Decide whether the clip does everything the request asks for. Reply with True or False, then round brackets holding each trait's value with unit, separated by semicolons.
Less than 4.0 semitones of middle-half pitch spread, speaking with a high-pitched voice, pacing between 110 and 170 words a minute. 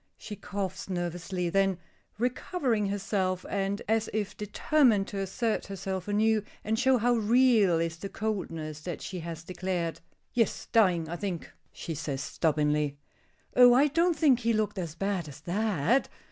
False (4.4 semitones; 195 Hz; 155 wpm)